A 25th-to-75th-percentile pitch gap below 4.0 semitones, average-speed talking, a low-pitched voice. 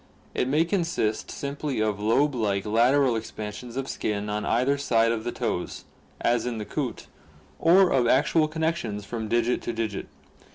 No: average, 4.5 semitones; average, 165 wpm; low, 120 Hz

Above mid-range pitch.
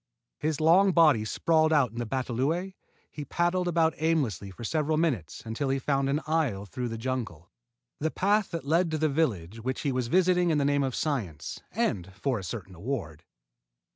No: medium, 140 Hz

